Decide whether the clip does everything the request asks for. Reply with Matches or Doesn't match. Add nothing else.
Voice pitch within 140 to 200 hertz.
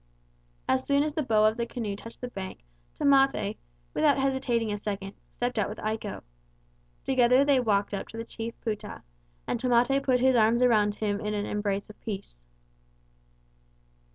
Doesn't match